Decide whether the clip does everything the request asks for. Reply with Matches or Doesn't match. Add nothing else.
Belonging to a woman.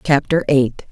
Matches